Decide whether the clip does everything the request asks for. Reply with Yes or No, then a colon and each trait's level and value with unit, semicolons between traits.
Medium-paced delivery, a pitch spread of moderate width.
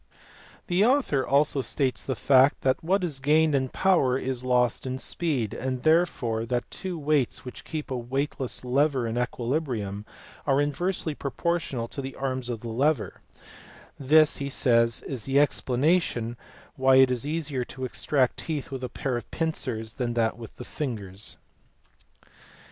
Yes: average, 160 wpm; average, 3.5 semitones